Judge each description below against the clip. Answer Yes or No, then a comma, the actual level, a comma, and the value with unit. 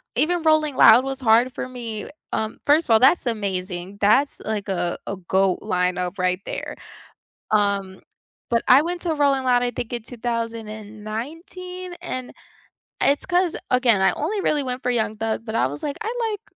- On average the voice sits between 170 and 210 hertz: No, high, 235 Hz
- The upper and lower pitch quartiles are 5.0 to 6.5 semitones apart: Yes, wide, 5.6 semitones